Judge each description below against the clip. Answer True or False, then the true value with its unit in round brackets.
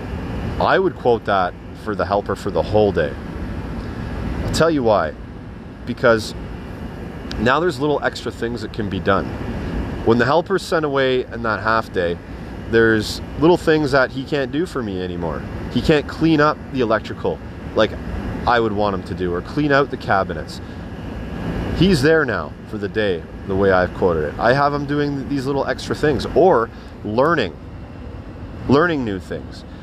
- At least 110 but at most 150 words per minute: False (175 wpm)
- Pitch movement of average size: False (6.9 semitones)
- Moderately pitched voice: False (105 Hz)